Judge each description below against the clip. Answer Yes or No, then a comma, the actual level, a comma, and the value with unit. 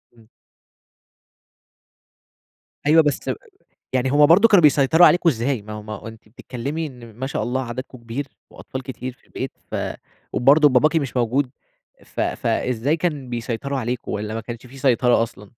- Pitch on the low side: Yes, low, 130 Hz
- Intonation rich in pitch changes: No, average, 3.6 semitones